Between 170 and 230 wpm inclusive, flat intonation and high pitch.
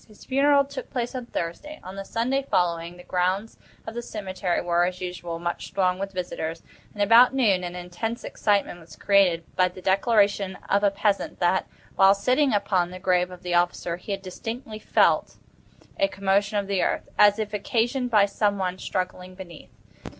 No: average, 185 wpm; average, 3.3 semitones; high, 195 Hz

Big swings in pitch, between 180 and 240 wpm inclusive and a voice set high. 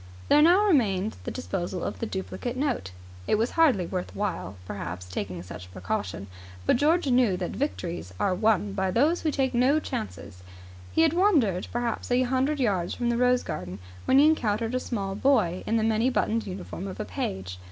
Yes: wide, 6.6 semitones; average, 195 wpm; high, 220 Hz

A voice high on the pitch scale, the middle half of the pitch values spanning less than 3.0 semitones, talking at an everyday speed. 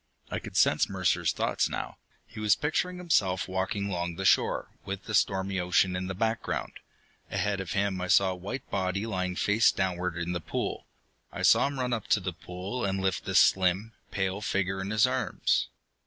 No: very low, 95 Hz; narrow, 2.5 semitones; average, 195 wpm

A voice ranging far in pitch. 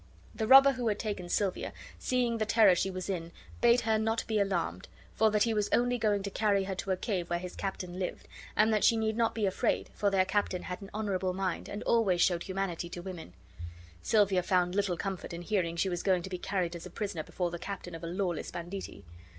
No: average, 3.2 semitones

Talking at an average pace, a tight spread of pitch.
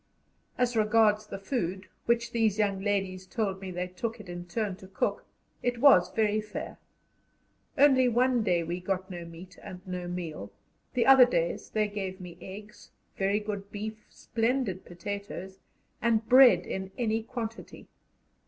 No: average, 155 wpm; average, 3.5 semitones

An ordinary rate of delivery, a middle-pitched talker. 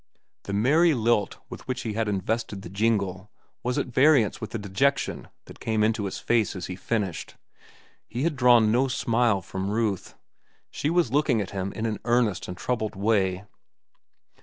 No: average, 175 wpm; low, 110 Hz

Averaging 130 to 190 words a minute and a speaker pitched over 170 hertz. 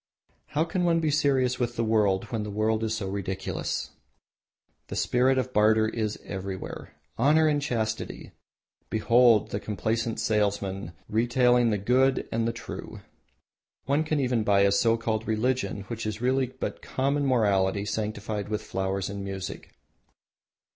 No: average, 150 wpm; low, 110 Hz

